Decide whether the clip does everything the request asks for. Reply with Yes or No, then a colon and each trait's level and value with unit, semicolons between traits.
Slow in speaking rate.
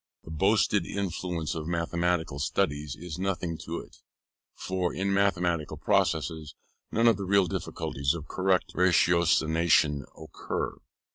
Yes: slow, 125 wpm